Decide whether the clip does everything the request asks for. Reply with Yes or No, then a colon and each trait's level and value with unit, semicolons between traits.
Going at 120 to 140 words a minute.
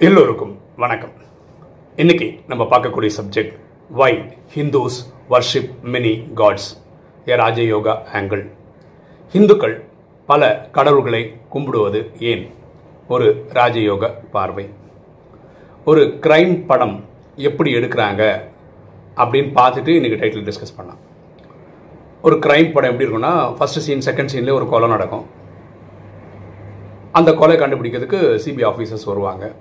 No: average, 105 wpm